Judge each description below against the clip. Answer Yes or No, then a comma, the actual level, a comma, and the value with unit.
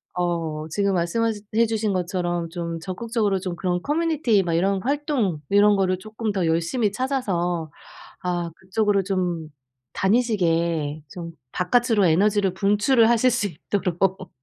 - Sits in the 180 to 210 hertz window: Yes, high, 190 Hz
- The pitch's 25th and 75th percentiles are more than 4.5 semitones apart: No, average, 4.0 semitones